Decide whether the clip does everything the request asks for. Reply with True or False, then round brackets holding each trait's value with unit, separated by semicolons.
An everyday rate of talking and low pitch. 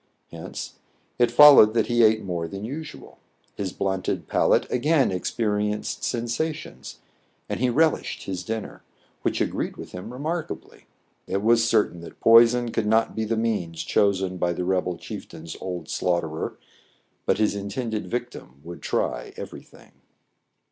True (155 wpm; 110 Hz)